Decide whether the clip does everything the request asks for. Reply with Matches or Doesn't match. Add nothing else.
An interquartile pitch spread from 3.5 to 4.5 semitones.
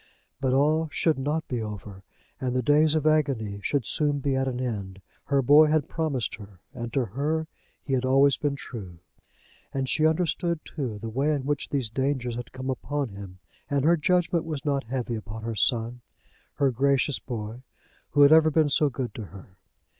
Matches